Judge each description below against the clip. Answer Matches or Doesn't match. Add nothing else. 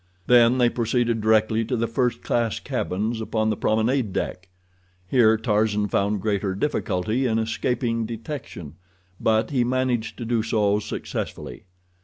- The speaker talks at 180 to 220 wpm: Doesn't match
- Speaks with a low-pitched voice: Matches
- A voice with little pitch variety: Matches